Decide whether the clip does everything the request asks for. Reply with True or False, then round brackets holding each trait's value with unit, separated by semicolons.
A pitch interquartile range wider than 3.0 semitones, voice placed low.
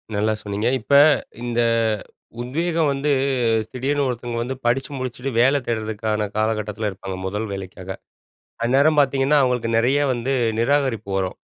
True (4.0 semitones; 120 Hz)